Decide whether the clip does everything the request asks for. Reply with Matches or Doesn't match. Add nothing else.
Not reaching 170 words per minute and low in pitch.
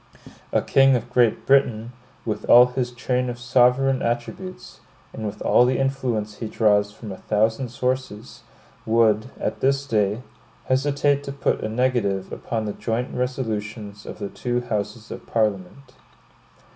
Matches